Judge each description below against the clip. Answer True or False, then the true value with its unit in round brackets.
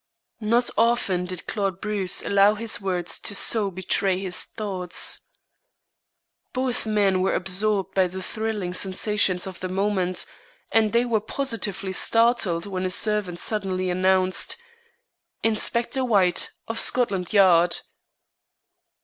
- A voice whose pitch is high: True (195 Hz)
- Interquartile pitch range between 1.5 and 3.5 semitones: True (2.9 semitones)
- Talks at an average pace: False (125 wpm)